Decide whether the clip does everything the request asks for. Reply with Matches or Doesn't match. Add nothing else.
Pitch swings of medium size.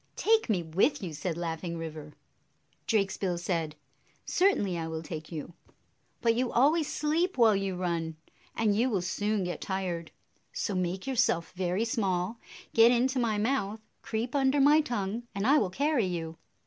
Doesn't match